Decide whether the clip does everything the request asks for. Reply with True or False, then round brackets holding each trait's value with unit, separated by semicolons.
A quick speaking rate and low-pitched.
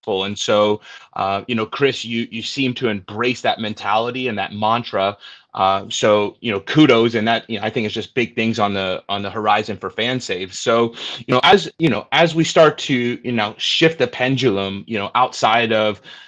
True (210 wpm; 115 Hz)